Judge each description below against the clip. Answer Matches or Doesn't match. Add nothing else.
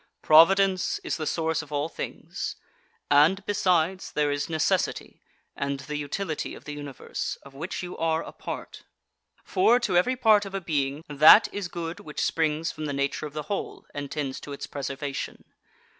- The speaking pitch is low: Doesn't match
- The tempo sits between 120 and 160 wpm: Doesn't match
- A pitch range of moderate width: Matches